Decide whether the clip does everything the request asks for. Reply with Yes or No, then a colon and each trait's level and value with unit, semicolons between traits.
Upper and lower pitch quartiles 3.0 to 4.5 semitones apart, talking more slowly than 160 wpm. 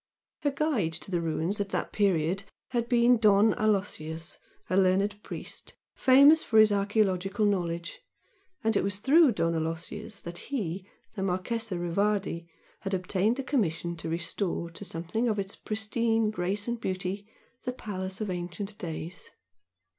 Yes: average, 3.8 semitones; average, 150 wpm